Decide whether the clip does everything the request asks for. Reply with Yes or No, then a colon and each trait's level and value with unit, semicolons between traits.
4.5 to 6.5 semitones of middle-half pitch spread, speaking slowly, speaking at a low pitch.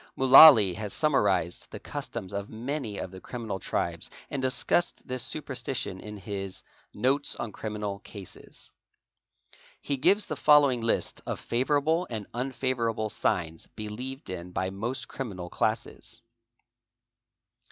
Yes: average, 4.9 semitones; slow, 130 wpm; low, 115 Hz